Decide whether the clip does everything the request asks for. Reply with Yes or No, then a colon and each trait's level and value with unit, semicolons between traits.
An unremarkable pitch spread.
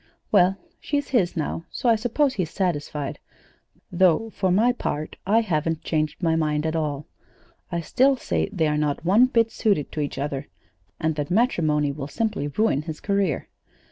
No: wide, 6.3 semitones